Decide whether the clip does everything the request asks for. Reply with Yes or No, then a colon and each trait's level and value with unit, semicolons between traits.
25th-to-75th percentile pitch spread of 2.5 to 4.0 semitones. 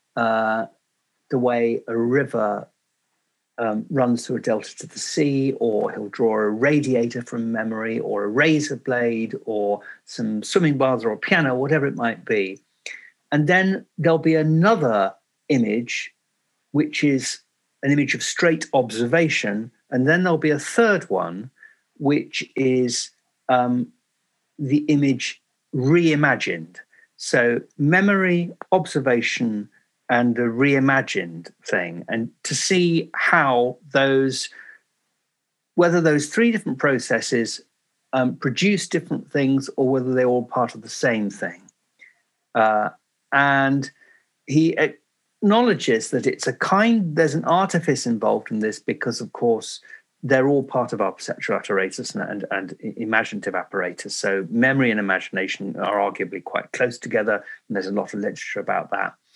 No: wide, 5.4 semitones